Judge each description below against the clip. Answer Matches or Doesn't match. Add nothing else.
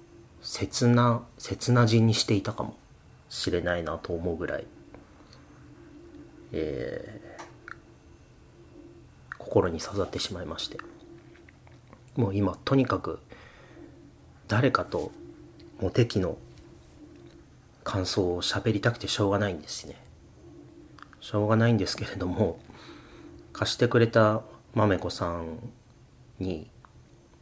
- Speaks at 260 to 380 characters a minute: Doesn't match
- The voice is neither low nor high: Doesn't match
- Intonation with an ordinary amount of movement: Matches